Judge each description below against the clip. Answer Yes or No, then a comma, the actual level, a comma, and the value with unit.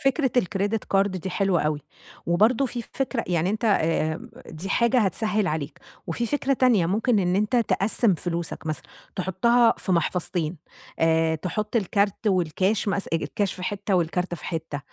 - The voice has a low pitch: No, high, 195 Hz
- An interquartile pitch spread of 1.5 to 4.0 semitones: No, average, 4.4 semitones